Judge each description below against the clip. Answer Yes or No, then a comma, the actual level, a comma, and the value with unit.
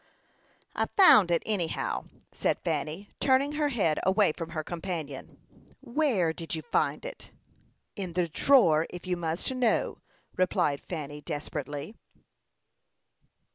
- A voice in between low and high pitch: Yes, medium, 175 Hz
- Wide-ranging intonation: Yes, wide, 6.0 semitones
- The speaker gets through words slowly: Yes, slow, 125 wpm